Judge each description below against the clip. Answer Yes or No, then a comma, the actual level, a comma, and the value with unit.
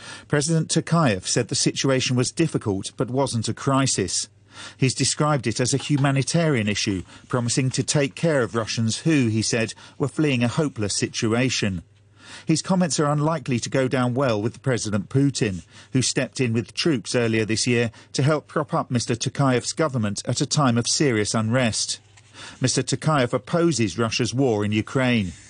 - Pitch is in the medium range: No, low, 125 Hz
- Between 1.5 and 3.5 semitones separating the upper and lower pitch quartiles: No, average, 4.3 semitones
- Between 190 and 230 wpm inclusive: No, average, 165 wpm